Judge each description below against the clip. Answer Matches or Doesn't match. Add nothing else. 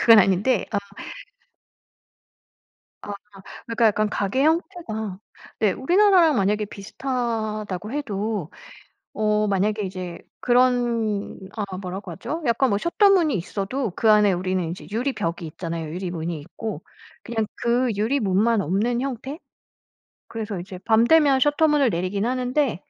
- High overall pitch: Matches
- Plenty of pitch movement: Doesn't match